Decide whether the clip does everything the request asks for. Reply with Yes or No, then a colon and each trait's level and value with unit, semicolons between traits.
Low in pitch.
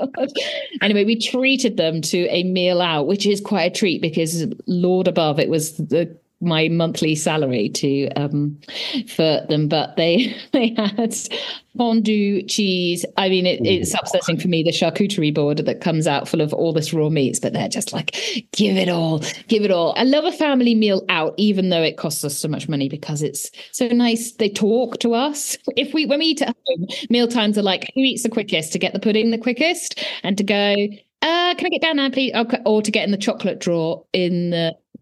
No: high, 200 Hz